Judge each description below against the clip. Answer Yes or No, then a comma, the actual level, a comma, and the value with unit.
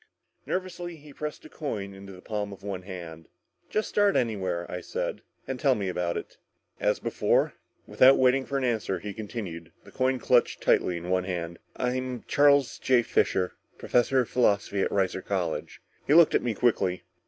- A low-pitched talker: Yes, low, 105 Hz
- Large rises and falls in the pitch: Yes, wide, 6.0 semitones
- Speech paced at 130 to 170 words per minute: No, average, 185 wpm